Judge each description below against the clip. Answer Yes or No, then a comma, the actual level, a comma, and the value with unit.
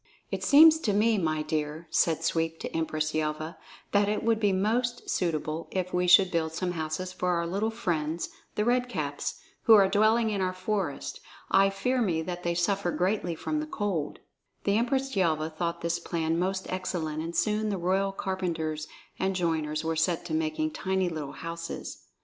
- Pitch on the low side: No, medium, 180 Hz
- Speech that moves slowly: No, average, 185 wpm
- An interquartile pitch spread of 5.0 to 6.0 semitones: No, average, 4.0 semitones